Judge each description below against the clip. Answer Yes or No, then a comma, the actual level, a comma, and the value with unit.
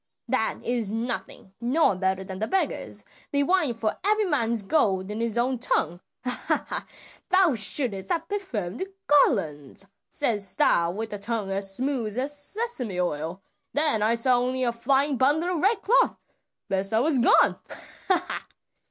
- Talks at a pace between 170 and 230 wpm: No, average, 160 wpm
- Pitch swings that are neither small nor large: No, wide, 6.7 semitones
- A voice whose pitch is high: Yes, high, 235 Hz